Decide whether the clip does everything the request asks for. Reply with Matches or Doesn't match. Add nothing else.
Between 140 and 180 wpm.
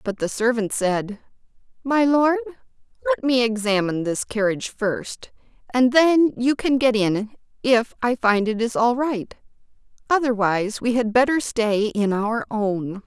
Matches